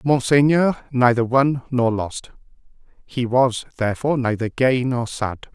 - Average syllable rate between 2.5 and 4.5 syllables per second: Yes, 4.3 syllables/s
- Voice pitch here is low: Yes, low, 125 Hz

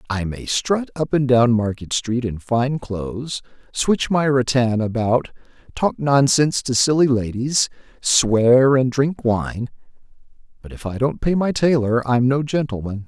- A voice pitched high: No, low, 125 Hz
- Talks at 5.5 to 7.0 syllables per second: No, 4.2 syllables/s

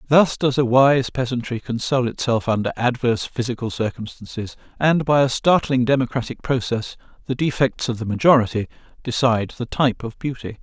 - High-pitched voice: No, low, 125 Hz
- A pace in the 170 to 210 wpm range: No, average, 150 wpm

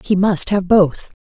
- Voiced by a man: No, female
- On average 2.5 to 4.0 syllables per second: Yes, 3.9 syllables/s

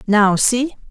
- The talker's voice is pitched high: Yes, high, 225 Hz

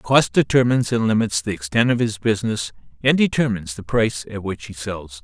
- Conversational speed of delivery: Yes, average, 195 wpm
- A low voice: Yes, low, 110 Hz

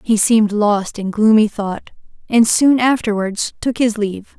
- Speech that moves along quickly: No, average, 165 wpm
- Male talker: No, female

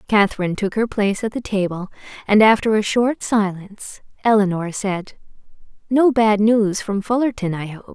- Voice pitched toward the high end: Yes, high, 210 Hz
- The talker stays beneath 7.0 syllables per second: Yes, 5.0 syllables/s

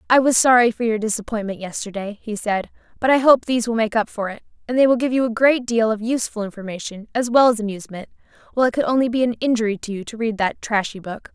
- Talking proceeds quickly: Yes, fast, 250 wpm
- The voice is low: No, high, 225 Hz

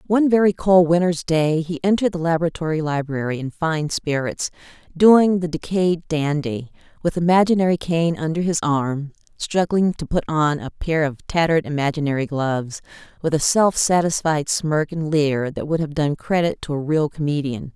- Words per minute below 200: Yes, average, 165 wpm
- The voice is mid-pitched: Yes, medium, 160 Hz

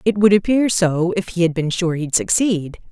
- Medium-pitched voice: Yes, medium, 180 Hz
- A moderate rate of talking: No, fast, 225 wpm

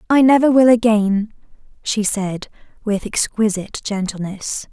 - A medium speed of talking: No, slow, 115 wpm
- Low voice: No, high, 215 Hz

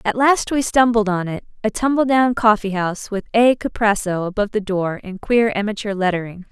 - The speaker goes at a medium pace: Yes, average, 185 wpm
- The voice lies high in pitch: Yes, high, 210 Hz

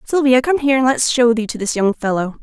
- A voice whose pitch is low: No, high, 245 Hz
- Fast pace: Yes, fast, 270 wpm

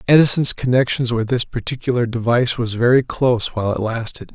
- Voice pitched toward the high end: No, low, 120 Hz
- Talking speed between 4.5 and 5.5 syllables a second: No, 6.1 syllables/s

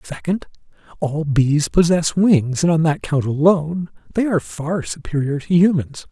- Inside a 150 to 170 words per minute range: Yes, average, 155 wpm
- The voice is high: No, medium, 155 Hz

